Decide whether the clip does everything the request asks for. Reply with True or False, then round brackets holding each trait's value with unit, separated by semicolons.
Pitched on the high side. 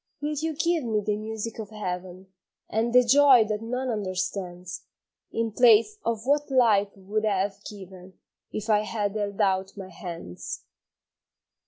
True (215 Hz)